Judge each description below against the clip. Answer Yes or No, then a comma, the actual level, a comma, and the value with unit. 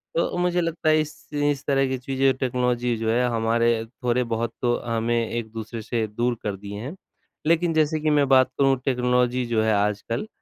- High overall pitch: No, low, 125 Hz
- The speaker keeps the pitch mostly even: No, average, 3.2 semitones